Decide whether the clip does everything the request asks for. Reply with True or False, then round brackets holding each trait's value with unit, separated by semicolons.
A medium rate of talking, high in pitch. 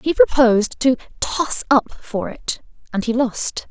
True (145 wpm; 255 Hz)